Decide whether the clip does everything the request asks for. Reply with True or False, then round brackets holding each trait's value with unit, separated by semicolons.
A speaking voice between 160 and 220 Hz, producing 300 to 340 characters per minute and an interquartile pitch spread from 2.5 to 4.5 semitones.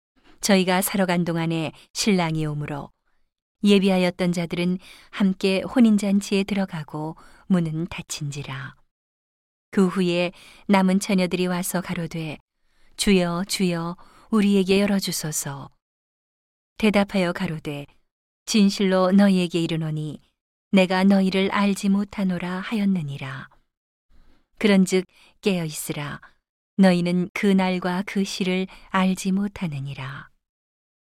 False (185 Hz; 240 characters per minute; 2.9 semitones)